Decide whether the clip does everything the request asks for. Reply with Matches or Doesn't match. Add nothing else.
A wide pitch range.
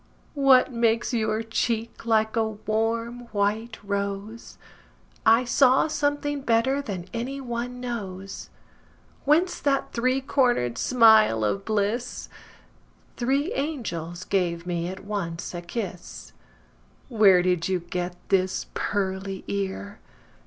Doesn't match